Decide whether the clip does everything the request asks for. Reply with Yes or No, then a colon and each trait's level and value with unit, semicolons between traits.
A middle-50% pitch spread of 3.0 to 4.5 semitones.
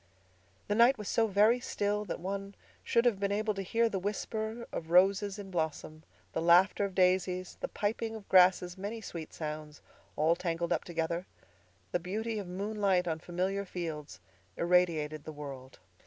Yes: average, 3.5 semitones